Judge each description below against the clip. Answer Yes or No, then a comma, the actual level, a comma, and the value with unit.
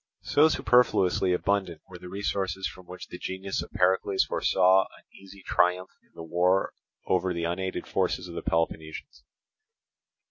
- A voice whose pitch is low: Yes, very low, 95 Hz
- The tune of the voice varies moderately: No, narrow, 1.5 semitones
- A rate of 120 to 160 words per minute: Yes, average, 150 wpm